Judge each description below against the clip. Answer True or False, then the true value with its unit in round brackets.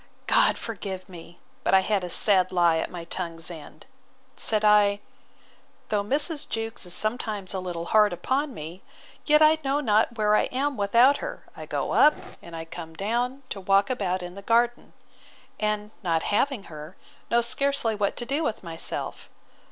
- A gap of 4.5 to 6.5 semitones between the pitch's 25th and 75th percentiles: True (5.0 semitones)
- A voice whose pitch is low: False (210 Hz)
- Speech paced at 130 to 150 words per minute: False (175 wpm)